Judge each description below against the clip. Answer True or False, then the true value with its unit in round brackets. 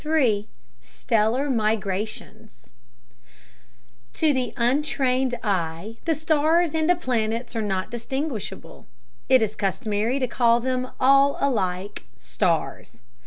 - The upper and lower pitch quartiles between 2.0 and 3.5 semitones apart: False (4.4 semitones)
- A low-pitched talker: False (240 Hz)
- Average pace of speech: False (110 wpm)